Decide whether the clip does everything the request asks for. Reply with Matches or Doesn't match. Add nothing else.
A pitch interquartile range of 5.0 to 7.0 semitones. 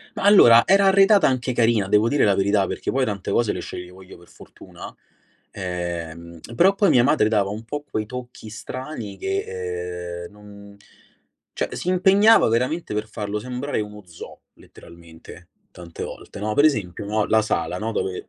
Matches